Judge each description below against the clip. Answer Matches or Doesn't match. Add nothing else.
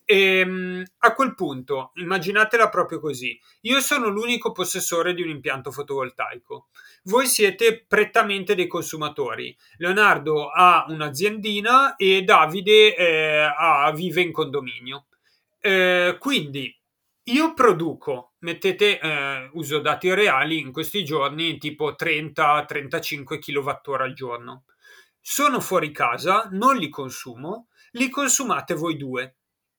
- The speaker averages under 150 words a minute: Matches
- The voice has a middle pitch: Matches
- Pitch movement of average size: Doesn't match